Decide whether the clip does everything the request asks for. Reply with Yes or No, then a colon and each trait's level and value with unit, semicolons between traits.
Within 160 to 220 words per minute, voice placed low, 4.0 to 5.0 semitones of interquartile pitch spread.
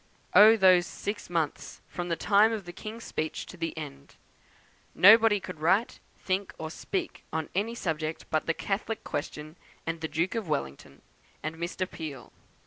No: average, 165 wpm; medium, 175 Hz; average, 4.5 semitones